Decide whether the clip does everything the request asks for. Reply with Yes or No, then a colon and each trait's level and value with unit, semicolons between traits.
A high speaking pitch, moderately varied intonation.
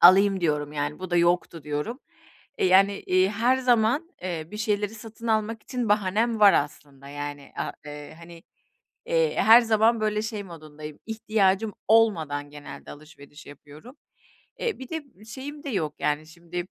No: high, 195 Hz; wide, 6.5 semitones